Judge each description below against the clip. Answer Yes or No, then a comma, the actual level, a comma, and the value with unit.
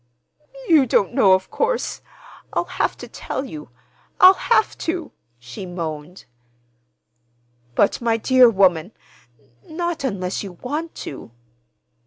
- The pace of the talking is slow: Yes, slow, 110 wpm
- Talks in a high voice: Yes, high, 195 Hz